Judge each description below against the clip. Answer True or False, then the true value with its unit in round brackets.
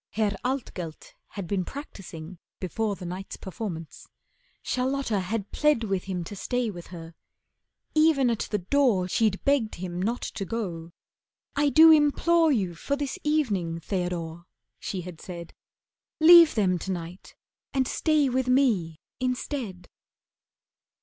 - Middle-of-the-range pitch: False (205 Hz)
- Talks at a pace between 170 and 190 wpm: False (135 wpm)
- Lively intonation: True (7.0 semitones)